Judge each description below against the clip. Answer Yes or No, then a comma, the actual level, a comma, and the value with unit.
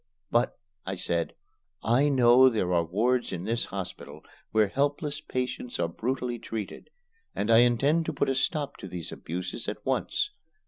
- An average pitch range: No, wide, 5.7 semitones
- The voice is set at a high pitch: No, low, 120 Hz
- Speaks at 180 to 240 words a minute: No, average, 165 wpm